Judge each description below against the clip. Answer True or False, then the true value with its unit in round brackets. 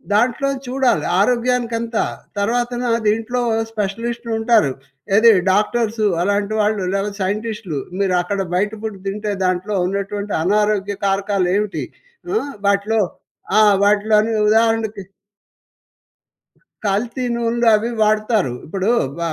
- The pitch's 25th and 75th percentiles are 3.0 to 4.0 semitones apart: False (2.4 semitones)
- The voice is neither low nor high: False (210 Hz)